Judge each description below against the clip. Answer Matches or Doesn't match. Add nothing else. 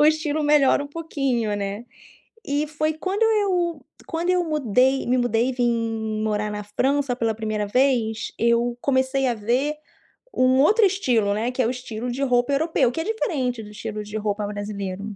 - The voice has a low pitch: Doesn't match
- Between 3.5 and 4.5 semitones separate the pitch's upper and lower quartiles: Doesn't match